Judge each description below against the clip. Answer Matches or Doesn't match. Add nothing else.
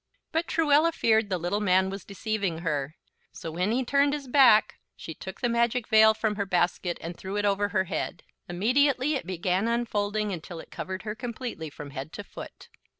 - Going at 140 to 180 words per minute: Doesn't match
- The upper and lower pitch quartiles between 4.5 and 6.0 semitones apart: Matches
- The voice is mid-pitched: Doesn't match